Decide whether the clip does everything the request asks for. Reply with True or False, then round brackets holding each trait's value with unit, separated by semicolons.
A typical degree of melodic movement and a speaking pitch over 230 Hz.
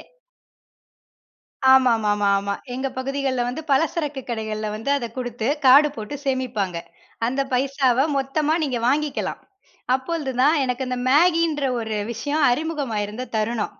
True (4.1 semitones; 260 Hz)